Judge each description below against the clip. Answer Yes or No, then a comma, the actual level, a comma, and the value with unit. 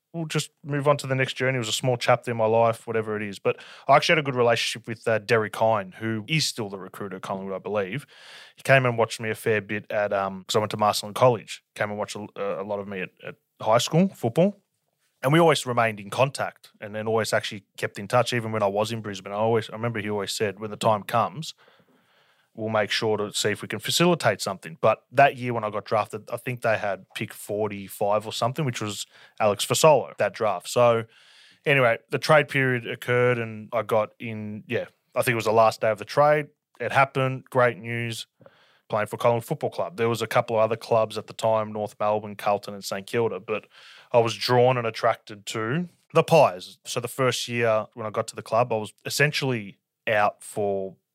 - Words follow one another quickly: Yes, fast, 230 wpm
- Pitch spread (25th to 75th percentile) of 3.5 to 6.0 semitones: No, average, 3.1 semitones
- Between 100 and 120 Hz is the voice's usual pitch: Yes, low, 115 Hz